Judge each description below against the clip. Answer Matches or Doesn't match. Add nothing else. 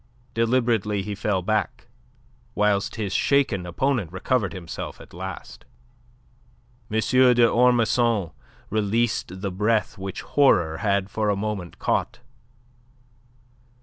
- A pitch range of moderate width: Matches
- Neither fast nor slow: Doesn't match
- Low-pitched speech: Matches